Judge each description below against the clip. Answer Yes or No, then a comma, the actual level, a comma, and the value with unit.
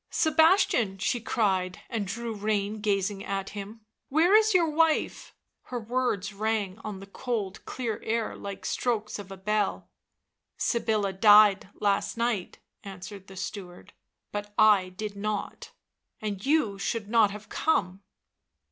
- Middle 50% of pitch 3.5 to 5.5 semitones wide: No, average, 2.8 semitones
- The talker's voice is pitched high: Yes, high, 210 Hz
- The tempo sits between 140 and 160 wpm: Yes, average, 155 wpm